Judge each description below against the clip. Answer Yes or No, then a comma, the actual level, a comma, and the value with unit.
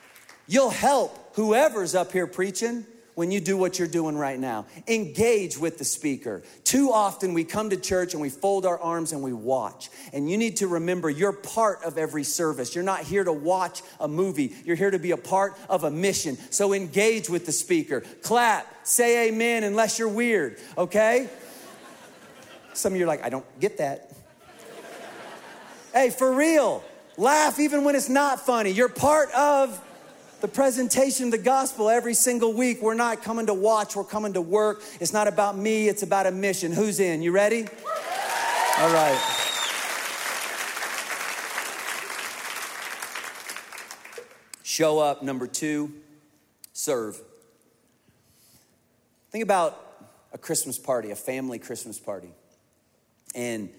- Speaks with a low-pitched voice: No, high, 205 Hz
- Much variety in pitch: Yes, wide, 5.8 semitones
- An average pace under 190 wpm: Yes, average, 155 wpm